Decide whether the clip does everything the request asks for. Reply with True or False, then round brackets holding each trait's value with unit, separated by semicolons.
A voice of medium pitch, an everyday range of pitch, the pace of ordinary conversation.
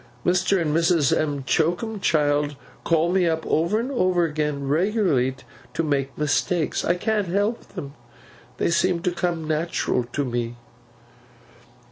False (165 Hz; 3.8 semitones; 130 wpm)